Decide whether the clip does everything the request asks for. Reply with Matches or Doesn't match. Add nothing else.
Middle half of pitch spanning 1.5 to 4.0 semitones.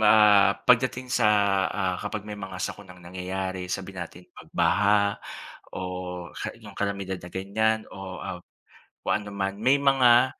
Matches